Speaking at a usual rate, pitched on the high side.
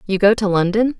No: fast, 240 wpm; high, 205 Hz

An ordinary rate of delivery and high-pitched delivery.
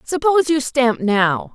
Yes: average, 155 wpm; very high, 260 Hz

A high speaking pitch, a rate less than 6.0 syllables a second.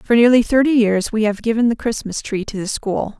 Yes: high, 225 Hz; 5.4 syllables/s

